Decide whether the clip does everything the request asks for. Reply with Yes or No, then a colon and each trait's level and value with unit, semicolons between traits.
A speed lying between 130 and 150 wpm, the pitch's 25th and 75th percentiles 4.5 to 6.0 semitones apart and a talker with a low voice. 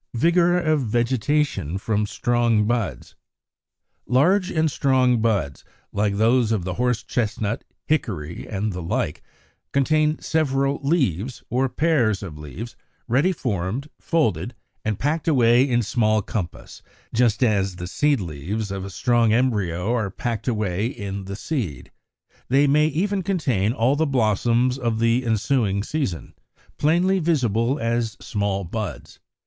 Yes: average, 140 wpm; average, 5.3 semitones; low, 115 Hz